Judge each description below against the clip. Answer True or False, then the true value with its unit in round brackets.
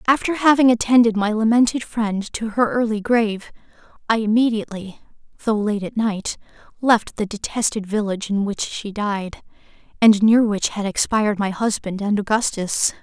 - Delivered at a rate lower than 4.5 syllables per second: False (4.9 syllables/s)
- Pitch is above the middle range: True (215 Hz)